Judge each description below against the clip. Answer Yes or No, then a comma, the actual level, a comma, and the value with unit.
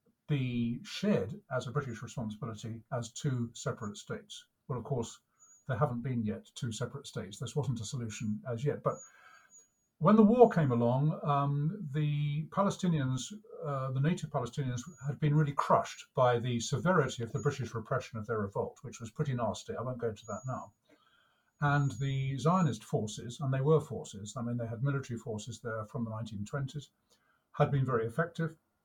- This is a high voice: No, low, 135 Hz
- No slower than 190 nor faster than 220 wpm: No, average, 175 wpm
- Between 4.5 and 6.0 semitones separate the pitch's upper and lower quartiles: No, average, 4.1 semitones